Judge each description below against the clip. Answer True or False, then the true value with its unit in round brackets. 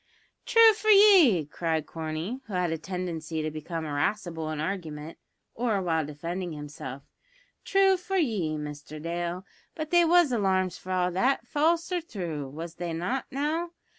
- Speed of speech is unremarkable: True (160 wpm)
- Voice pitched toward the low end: False (180 Hz)